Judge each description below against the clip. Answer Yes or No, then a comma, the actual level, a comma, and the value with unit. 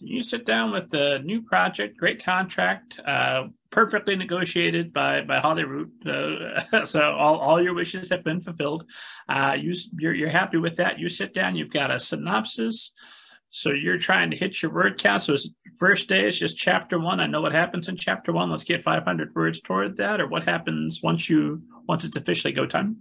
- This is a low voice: No, medium, 165 Hz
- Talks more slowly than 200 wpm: No, fast, 205 wpm